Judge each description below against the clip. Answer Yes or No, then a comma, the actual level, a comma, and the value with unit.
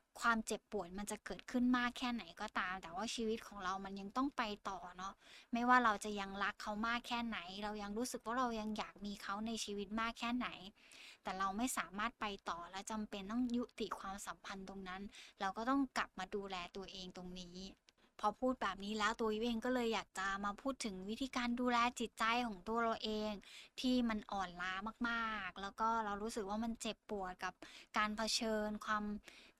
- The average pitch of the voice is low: No, high, 215 Hz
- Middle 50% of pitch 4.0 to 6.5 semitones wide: No, average, 3.0 semitones